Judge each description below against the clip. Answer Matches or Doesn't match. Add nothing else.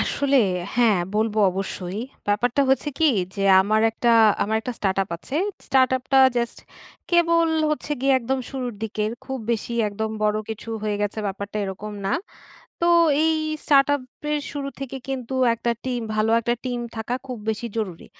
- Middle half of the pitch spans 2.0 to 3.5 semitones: Doesn't match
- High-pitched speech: Matches